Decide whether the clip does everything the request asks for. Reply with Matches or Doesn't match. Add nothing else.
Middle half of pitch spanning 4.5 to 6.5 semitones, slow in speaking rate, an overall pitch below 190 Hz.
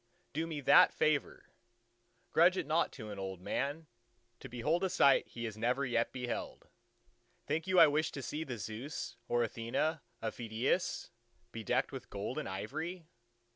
Doesn't match